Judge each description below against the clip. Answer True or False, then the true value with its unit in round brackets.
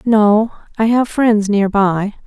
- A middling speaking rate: True (160 wpm)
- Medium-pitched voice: False (215 Hz)